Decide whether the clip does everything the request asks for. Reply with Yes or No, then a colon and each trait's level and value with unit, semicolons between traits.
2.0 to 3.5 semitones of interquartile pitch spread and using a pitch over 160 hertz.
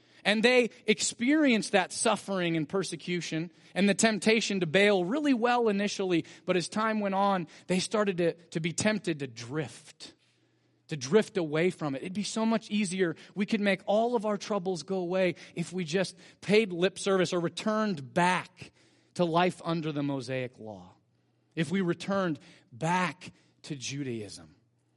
No: average, 3.9 semitones; medium, 185 Hz